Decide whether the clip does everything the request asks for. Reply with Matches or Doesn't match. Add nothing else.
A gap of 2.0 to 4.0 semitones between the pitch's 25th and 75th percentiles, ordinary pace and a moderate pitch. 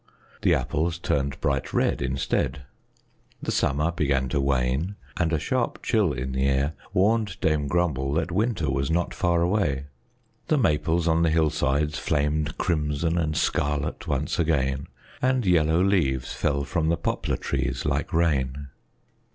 Doesn't match